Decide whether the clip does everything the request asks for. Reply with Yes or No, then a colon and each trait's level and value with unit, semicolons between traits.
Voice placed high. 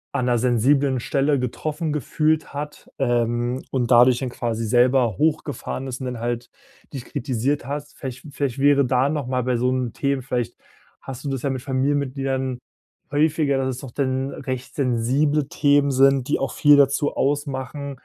No: low, 135 Hz